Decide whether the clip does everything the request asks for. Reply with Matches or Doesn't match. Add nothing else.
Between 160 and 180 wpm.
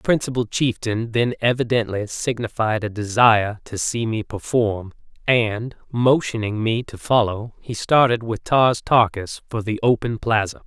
Doesn't match